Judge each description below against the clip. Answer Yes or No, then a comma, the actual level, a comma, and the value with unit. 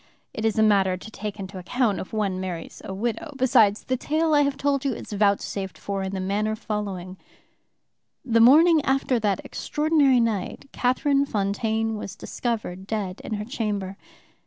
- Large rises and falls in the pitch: No, average, 4.7 semitones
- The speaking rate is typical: Yes, average, 170 wpm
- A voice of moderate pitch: No, high, 215 Hz